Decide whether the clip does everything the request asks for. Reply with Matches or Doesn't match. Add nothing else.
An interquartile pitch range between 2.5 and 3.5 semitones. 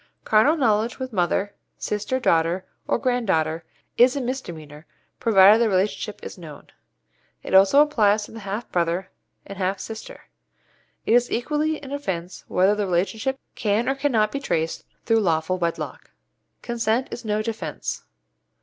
Doesn't match